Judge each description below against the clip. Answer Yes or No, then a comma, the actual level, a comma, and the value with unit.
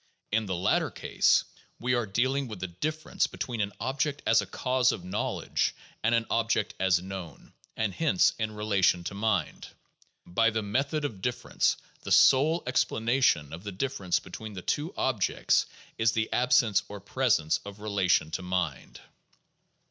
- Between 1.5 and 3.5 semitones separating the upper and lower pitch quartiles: No, average, 5.0 semitones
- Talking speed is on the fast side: No, average, 165 wpm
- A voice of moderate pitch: No, low, 110 Hz